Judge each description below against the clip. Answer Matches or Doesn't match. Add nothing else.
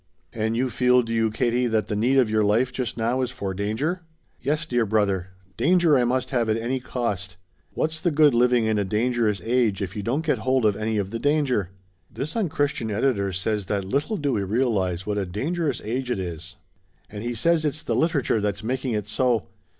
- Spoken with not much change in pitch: Doesn't match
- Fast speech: Matches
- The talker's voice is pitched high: Doesn't match